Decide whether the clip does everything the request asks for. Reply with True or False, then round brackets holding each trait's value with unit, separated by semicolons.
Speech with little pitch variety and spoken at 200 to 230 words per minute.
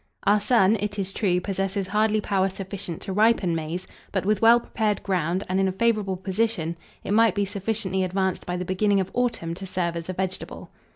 True (2.3 semitones; 205 wpm)